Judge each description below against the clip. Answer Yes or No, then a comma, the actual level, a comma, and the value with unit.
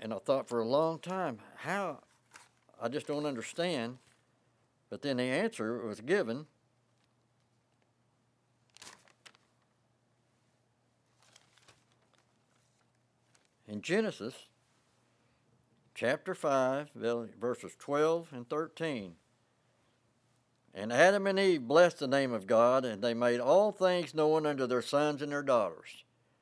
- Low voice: Yes, low, 125 Hz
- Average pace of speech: No, slow, 105 wpm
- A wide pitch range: No, average, 4.0 semitones